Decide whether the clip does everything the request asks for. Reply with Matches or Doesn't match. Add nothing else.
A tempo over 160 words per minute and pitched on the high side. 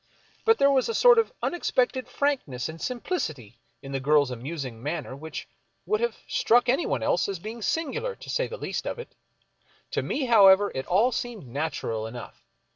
Matches